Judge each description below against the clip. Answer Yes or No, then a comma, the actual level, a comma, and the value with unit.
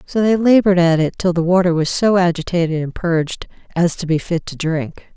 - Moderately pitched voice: Yes, medium, 175 Hz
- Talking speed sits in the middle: No, fast, 220 wpm